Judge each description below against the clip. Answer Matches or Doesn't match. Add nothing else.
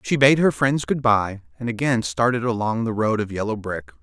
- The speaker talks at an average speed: Doesn't match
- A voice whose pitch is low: Matches